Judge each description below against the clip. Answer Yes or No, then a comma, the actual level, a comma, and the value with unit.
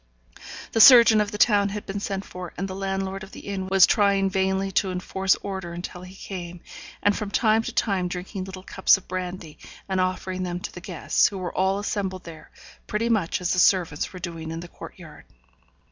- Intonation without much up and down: Yes, narrow, 1.7 semitones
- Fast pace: Yes, fast, 210 wpm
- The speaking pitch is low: No, high, 190 Hz